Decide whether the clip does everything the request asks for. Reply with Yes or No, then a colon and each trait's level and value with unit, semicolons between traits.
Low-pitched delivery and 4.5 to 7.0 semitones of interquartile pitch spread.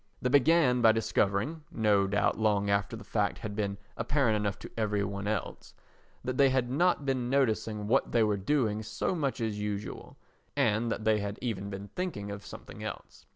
No: low, 110 Hz; average, 3.7 semitones